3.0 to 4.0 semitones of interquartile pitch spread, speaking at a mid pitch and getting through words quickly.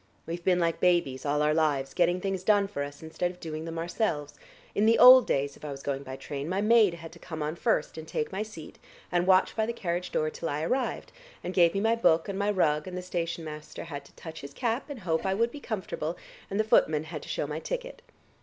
No: average, 4.5 semitones; medium, 170 Hz; fast, 255 wpm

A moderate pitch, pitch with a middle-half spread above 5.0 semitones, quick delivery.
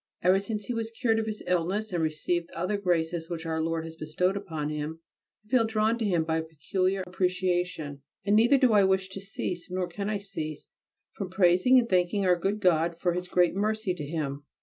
No: medium, 180 Hz; average, 3.8 semitones; fast, 215 wpm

